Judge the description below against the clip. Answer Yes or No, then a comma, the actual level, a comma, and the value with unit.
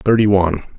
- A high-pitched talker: No, low, 100 Hz